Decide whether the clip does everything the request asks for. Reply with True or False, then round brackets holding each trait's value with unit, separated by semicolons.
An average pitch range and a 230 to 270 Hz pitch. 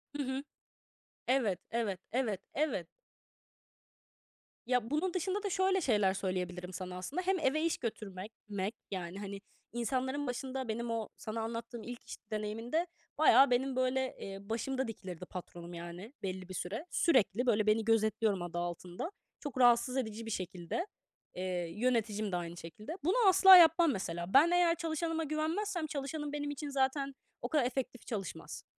False (6.7 semitones; 235 Hz)